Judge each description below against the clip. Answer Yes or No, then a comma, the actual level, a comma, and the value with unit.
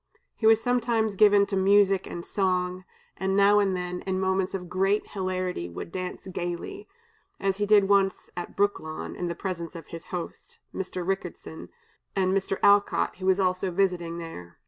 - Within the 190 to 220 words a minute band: No, average, 170 wpm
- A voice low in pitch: No, high, 190 Hz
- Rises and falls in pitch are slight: Yes, narrow, 1.8 semitones